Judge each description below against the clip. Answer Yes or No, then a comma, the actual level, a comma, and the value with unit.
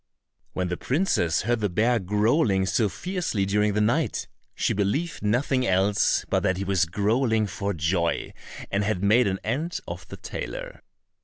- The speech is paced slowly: No, average, 165 wpm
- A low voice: Yes, low, 105 Hz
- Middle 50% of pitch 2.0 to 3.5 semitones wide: No, average, 4.1 semitones